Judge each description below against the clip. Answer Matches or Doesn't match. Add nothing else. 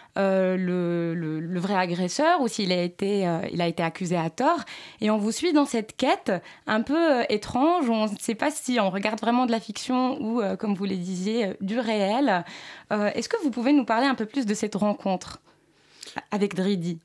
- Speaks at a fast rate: Matches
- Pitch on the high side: Matches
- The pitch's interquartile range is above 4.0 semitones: Matches